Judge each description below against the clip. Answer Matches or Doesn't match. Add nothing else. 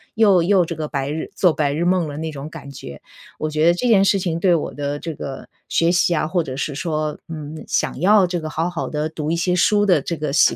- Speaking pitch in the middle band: Matches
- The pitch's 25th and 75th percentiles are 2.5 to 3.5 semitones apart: Matches